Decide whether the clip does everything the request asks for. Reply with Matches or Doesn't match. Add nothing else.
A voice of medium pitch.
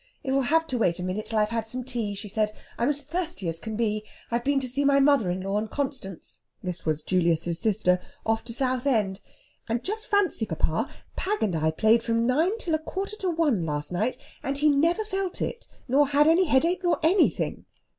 Doesn't match